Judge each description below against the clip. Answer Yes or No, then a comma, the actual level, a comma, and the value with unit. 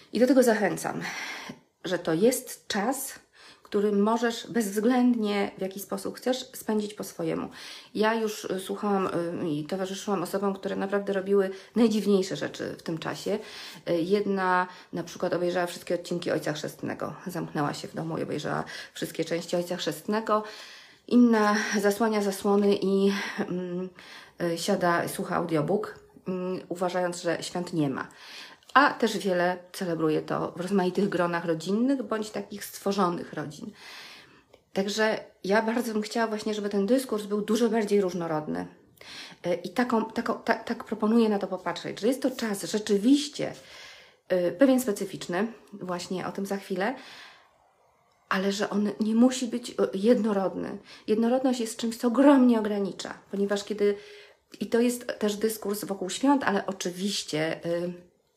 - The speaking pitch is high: Yes, high, 200 Hz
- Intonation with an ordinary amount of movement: Yes, average, 3.6 semitones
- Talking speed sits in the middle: Yes, average, 140 wpm